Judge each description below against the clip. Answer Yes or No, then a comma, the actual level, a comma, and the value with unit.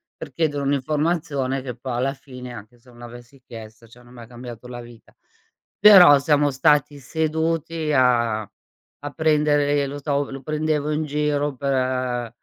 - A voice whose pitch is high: No, low, 135 Hz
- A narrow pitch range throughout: No, average, 3.5 semitones